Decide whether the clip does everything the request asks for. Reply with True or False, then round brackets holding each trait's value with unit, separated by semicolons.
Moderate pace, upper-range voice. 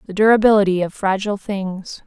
True (145 wpm; 200 Hz)